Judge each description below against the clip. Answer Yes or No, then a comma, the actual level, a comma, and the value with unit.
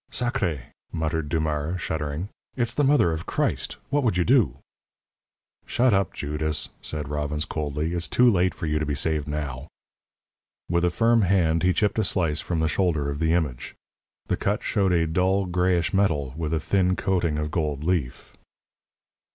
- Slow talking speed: No, average, 175 wpm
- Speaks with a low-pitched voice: Yes, very low, 80 Hz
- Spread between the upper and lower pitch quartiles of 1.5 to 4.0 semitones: Yes, average, 3.6 semitones